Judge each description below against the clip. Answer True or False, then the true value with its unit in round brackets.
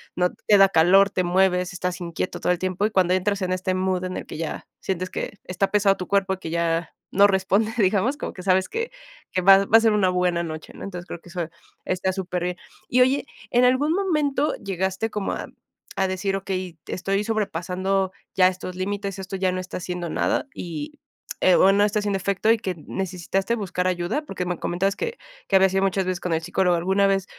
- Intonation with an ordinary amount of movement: False (1.7 semitones)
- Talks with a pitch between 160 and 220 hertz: True (190 Hz)